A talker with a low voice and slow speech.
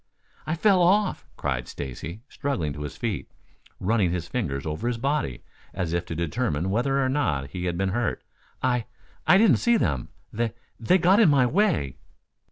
No: low, 110 Hz; average, 175 wpm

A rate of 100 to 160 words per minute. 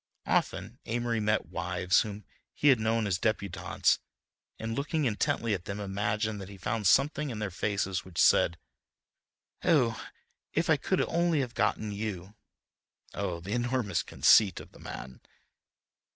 Yes: average, 150 wpm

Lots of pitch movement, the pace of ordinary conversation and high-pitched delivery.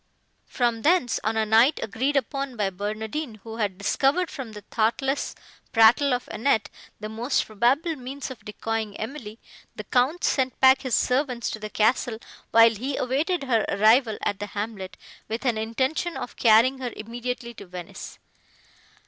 No: average, 3.5 semitones; average, 160 wpm; high, 235 Hz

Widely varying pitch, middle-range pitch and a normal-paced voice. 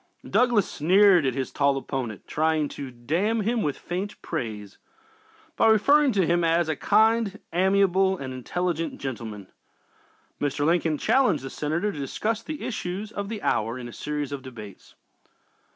Yes: wide, 7.0 semitones; medium, 165 Hz; average, 155 wpm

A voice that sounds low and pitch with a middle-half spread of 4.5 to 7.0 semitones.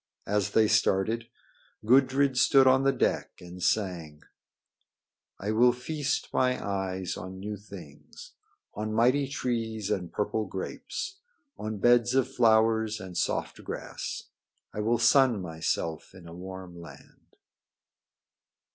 Yes: low, 110 Hz; average, 4.8 semitones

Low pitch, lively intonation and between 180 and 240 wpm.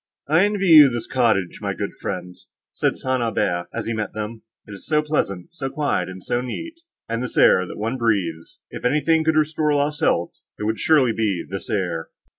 Yes: low, 120 Hz; wide, 7.4 semitones; average, 200 wpm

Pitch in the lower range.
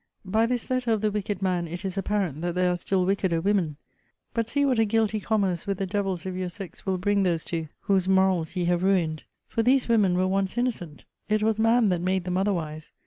No: high, 190 Hz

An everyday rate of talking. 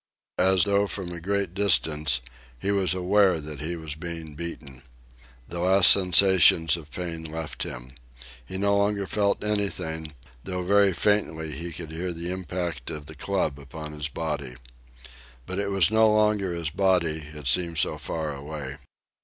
Yes: average, 160 wpm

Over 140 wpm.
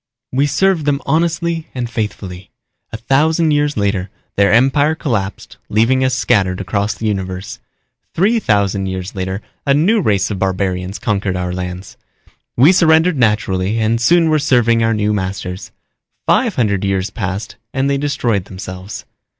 Yes: average, 150 wpm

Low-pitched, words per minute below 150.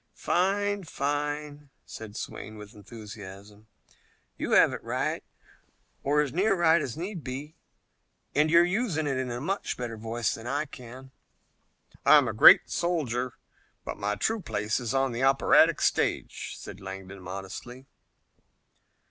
Yes: low, 130 Hz; average, 140 wpm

